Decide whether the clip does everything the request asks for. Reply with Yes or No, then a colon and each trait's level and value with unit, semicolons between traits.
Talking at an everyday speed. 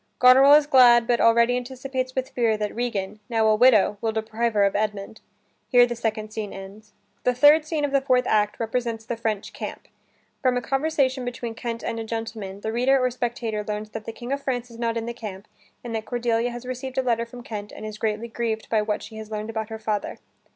No: fast, 230 wpm